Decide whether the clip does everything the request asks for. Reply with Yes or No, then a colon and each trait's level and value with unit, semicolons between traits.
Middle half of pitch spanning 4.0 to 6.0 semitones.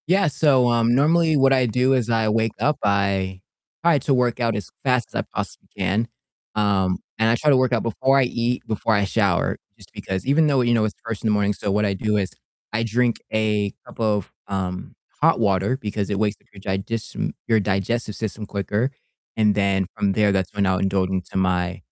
No: average, 3.6 semitones